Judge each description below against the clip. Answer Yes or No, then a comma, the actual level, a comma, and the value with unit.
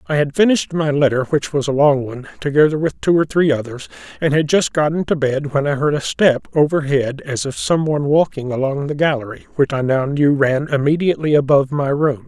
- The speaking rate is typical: No, fast, 215 wpm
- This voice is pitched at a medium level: Yes, medium, 145 Hz